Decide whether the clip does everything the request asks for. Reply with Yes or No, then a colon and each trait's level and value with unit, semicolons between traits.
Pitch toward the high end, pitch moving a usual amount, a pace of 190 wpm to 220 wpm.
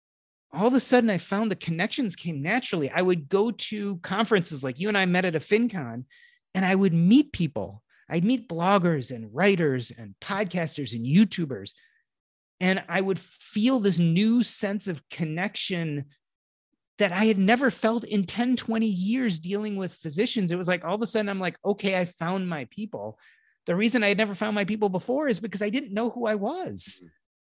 Yes: high, 195 Hz; average, 4.4 semitones; average, 195 wpm